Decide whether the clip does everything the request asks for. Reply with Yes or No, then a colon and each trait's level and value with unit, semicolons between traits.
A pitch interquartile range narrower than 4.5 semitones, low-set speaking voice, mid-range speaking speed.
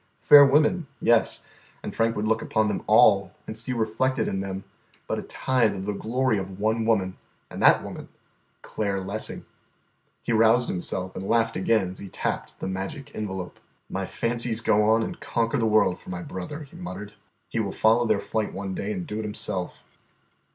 Yes: average, 3.1 semitones; low, 110 Hz; average, 190 wpm